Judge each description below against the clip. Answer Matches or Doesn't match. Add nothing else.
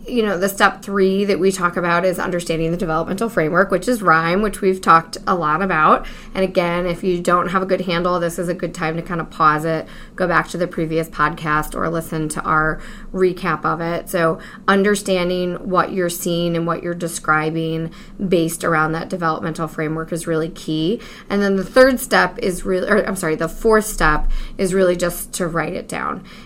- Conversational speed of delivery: Doesn't match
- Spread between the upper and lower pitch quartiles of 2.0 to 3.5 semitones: Matches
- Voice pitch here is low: Doesn't match